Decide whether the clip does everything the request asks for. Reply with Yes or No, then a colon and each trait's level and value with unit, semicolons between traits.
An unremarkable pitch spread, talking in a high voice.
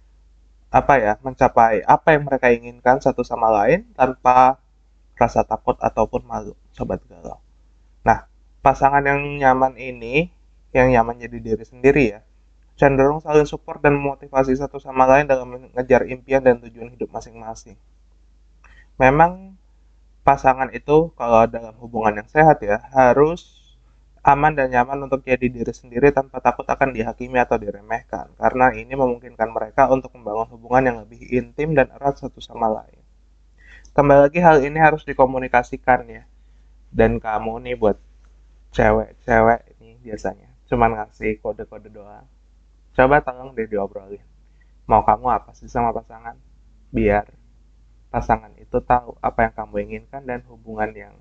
No: average, 3.6 semitones; low, 120 Hz